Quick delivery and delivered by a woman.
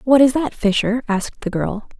Yes: fast, 210 wpm; female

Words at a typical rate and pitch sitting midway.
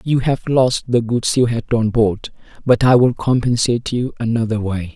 No: average, 195 wpm; low, 120 Hz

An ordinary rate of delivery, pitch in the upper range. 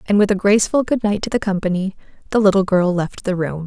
No: fast, 245 wpm; high, 195 Hz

